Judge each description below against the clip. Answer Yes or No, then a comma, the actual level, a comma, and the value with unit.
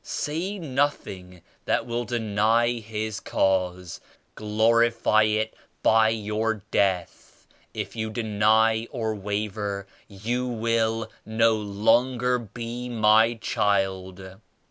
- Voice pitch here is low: Yes, low, 110 Hz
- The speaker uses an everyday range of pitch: No, narrow, 2.2 semitones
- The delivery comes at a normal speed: No, slow, 100 wpm